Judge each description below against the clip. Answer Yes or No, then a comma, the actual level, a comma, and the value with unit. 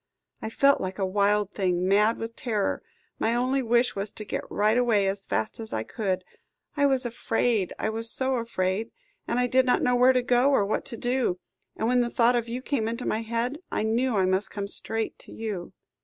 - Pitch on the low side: No, high, 225 Hz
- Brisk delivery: Yes, fast, 220 wpm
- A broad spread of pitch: No, average, 3.5 semitones